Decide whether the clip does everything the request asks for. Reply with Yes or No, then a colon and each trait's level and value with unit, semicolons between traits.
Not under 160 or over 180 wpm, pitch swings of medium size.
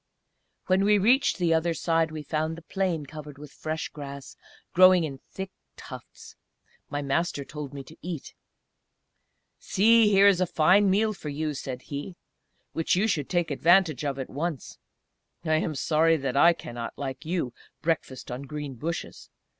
Yes: average, 165 wpm; average, 4.0 semitones